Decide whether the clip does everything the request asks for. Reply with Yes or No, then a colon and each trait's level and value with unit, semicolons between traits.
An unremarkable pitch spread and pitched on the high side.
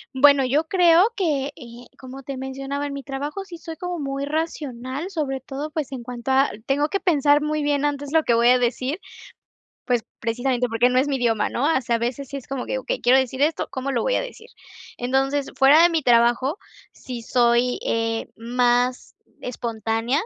Yes: average, 3.1 semitones; very high, 270 Hz